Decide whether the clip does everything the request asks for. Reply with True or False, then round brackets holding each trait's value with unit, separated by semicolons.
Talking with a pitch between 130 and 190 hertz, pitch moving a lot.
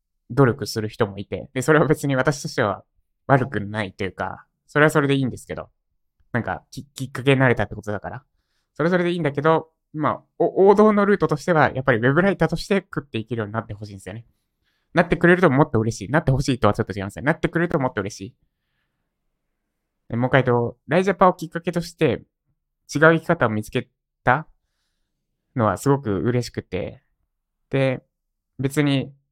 True (135 Hz; 6.1 semitones)